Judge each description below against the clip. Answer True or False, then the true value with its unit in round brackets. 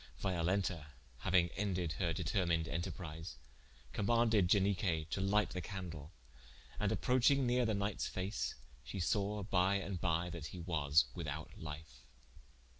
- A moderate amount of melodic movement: True (3.4 semitones)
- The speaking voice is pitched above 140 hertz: False (90 Hz)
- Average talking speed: False (130 wpm)